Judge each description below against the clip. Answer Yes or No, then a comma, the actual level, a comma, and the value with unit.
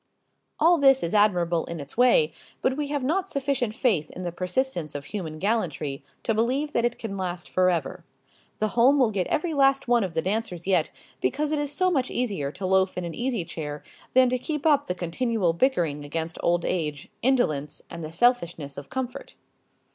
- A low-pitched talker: No, high, 205 Hz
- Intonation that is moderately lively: No, wide, 7.6 semitones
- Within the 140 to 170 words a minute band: No, average, 195 wpm